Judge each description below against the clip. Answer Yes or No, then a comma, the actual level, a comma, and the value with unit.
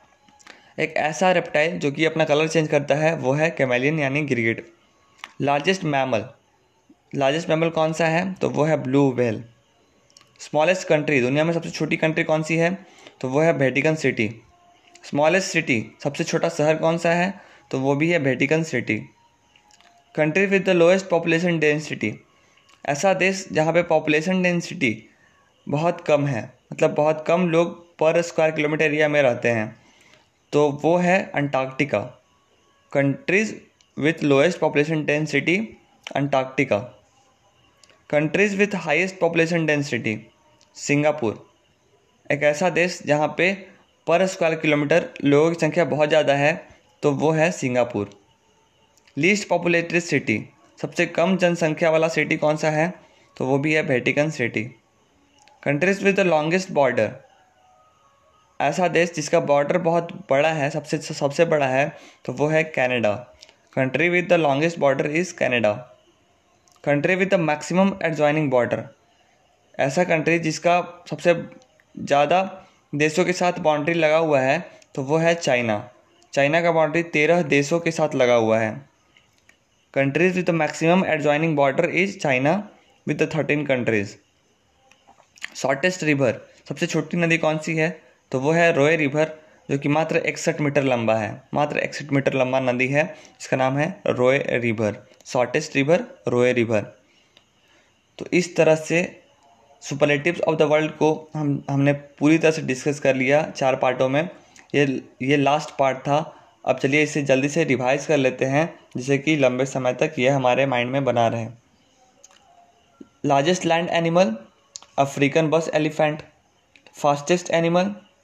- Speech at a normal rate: Yes, average, 150 wpm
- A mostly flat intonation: No, average, 3.4 semitones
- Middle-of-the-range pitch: Yes, medium, 155 Hz